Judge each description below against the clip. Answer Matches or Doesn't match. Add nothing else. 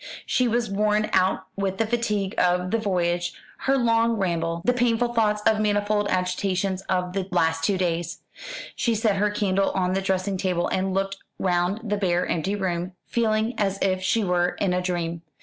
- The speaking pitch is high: Matches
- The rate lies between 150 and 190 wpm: Matches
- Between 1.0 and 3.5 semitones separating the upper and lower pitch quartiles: Matches